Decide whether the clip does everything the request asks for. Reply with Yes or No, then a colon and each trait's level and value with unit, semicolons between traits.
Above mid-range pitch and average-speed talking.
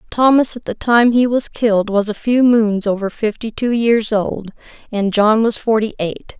Yes: high, 220 Hz; average, 195 wpm